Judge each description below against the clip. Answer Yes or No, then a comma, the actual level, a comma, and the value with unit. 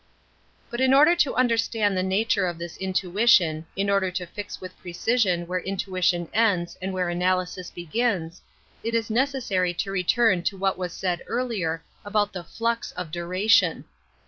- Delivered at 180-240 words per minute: No, average, 165 wpm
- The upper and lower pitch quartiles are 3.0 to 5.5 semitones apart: Yes, average, 4.0 semitones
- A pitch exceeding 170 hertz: Yes, high, 190 Hz